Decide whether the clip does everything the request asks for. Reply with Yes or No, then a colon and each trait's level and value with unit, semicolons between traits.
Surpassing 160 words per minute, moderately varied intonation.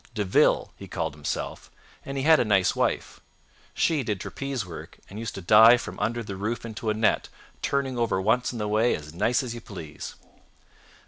Yes: average, 200 wpm; average, 3.7 semitones